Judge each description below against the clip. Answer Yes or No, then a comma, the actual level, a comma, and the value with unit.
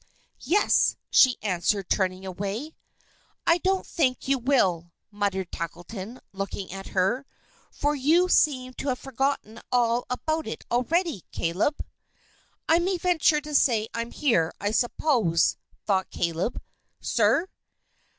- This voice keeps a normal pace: No, slow, 125 wpm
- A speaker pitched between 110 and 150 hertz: No, high, 240 Hz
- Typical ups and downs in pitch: No, wide, 7.4 semitones